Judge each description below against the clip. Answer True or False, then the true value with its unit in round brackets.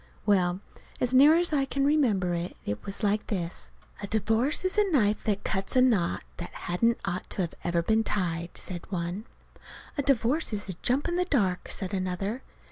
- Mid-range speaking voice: False (210 Hz)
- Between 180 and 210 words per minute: True (185 wpm)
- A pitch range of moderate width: False (6.2 semitones)